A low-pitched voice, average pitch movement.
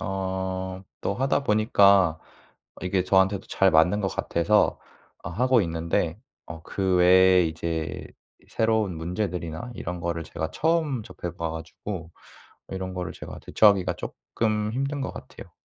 Yes: very low, 95 Hz; average, 3.8 semitones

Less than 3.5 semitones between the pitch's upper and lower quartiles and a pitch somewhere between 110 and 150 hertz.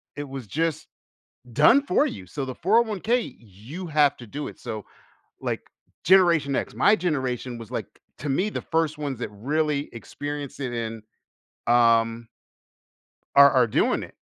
No: average, 5.2 semitones; medium, 140 Hz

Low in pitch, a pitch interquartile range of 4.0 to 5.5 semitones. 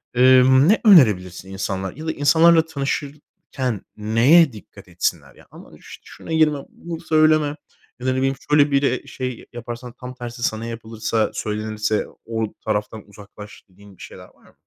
Yes: low, 125 Hz; average, 5.2 semitones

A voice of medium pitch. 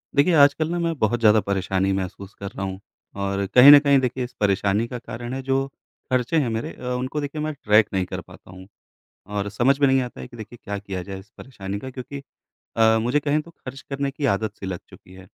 No: low, 120 Hz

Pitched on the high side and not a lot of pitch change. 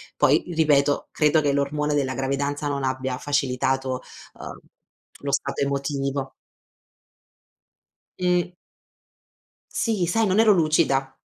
No: medium, 140 Hz; narrow, 2.3 semitones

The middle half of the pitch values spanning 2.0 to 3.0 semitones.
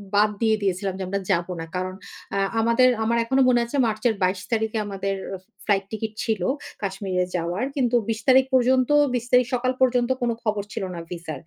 No: average, 4.0 semitones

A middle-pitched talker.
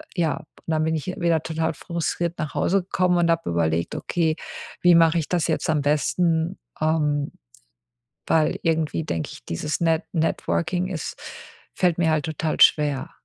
Yes: medium, 160 Hz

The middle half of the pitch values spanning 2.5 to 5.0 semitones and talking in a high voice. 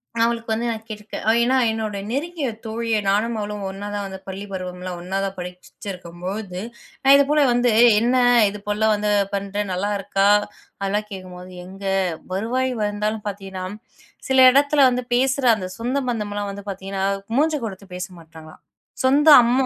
Yes: average, 3.7 semitones; high, 210 Hz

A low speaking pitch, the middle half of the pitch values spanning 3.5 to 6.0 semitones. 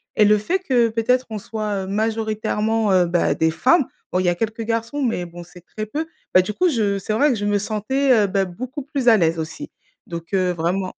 No: high, 215 Hz; average, 4.0 semitones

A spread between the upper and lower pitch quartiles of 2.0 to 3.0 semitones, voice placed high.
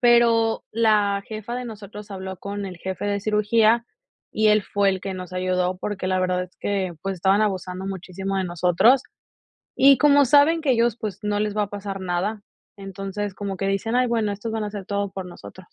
Yes: narrow, 2.5 semitones; high, 200 Hz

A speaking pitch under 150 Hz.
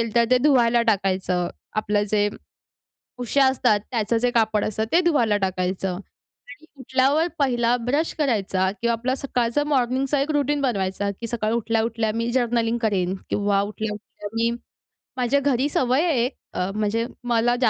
No: high, 235 Hz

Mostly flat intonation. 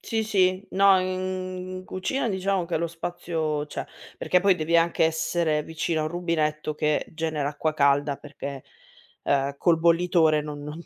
No: average, 3.3 semitones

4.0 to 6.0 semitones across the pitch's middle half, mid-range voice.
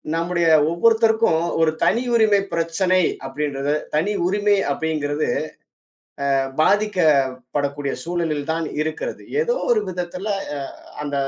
Yes: wide, 5.6 semitones; medium, 165 Hz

